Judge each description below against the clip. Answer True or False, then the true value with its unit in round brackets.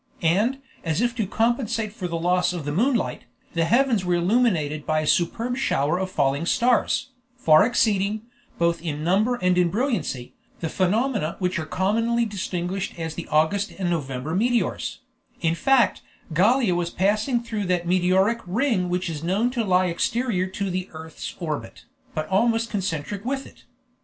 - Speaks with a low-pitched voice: False (185 Hz)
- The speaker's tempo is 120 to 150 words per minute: False (165 wpm)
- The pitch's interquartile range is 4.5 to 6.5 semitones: True (5.3 semitones)